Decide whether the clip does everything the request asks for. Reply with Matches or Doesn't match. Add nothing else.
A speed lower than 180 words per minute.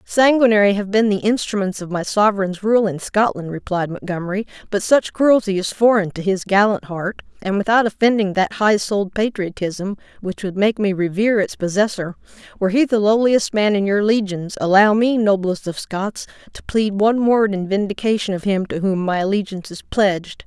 Doesn't match